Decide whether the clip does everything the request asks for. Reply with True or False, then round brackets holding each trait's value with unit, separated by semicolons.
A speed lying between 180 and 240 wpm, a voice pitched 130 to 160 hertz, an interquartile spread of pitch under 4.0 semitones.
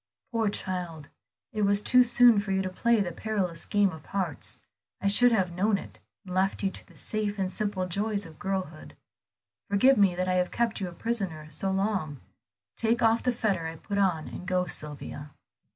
False (200 wpm; 195 Hz; 3.1 semitones)